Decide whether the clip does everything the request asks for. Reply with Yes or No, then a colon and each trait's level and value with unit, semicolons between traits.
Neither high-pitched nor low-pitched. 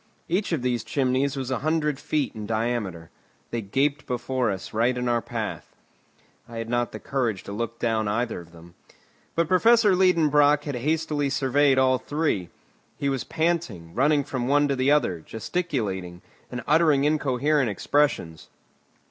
No: low, 130 Hz